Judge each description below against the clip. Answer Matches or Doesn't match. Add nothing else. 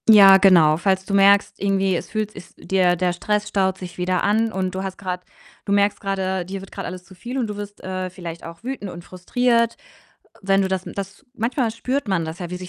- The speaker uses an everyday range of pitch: Doesn't match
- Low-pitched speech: Doesn't match